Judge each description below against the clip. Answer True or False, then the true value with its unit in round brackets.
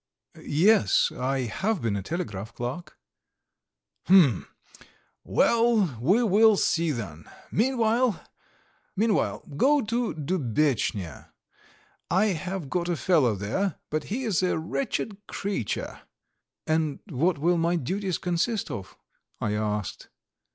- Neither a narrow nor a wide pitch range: False (7.7 semitones)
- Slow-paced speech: True (110 wpm)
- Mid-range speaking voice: True (175 Hz)